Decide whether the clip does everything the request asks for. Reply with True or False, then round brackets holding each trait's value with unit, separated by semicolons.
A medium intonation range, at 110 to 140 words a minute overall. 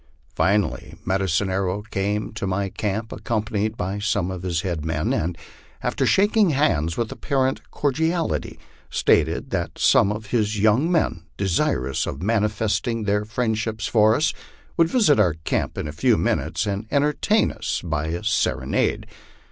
False (3.9 semitones; 155 wpm)